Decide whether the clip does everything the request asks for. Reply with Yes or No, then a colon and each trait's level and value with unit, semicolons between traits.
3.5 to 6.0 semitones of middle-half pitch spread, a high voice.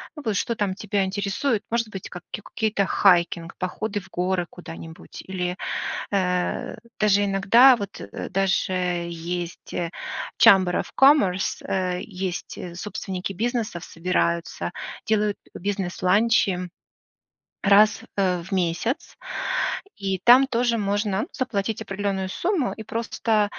No: average, 3.1 semitones; high, 195 Hz